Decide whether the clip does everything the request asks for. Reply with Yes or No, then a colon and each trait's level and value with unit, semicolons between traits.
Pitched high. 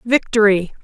Yes: high, 210 Hz